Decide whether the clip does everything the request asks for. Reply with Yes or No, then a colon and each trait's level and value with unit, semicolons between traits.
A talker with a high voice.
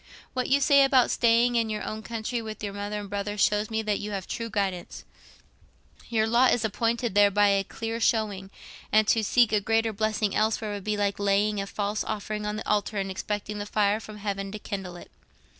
Yes: high, 210 Hz